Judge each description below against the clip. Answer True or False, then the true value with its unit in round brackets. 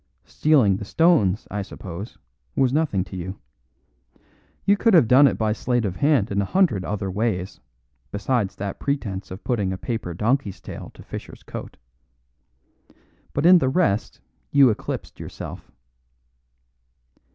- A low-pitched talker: True (110 Hz)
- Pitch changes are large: True (6.3 semitones)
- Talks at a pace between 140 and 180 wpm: True (145 wpm)